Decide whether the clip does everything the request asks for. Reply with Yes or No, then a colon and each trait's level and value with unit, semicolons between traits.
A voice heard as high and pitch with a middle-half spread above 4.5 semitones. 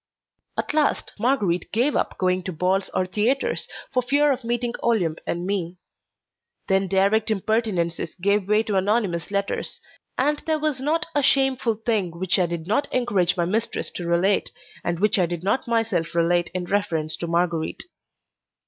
Yes: high, 200 Hz; average, 5.1 semitones